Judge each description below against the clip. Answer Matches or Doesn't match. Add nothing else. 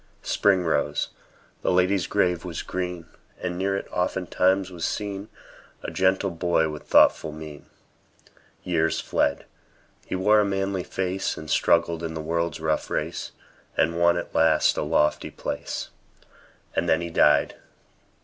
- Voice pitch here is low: Matches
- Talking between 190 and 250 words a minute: Doesn't match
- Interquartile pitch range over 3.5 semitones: Doesn't match